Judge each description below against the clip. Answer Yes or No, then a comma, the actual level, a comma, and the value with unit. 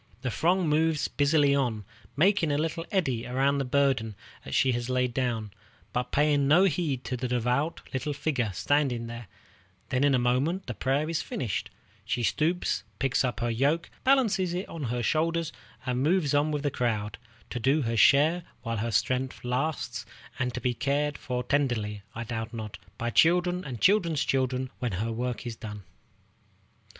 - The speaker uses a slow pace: No, average, 175 wpm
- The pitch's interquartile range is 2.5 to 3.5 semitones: No, average, 4.2 semitones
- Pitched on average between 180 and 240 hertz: No, low, 130 Hz